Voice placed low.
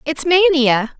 No: very high, 295 Hz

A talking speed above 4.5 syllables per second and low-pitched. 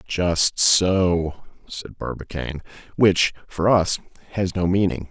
No: 3.6 syllables/s; very low, 90 Hz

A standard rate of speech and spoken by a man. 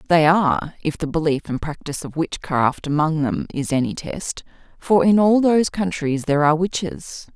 No: average, 180 wpm; female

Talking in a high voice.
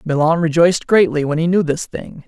No: medium, 165 Hz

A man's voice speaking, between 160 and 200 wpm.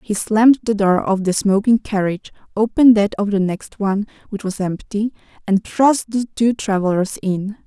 No: female; average, 180 wpm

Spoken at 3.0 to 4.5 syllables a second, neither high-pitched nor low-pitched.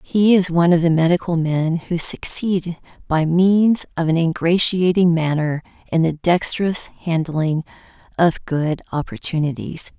Yes: 4.3 syllables/s; medium, 170 Hz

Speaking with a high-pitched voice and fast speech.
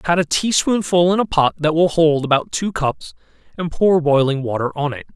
No: medium, 160 Hz; fast, 220 wpm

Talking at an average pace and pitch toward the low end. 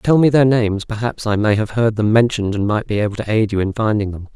No: fast, 290 wpm; low, 110 Hz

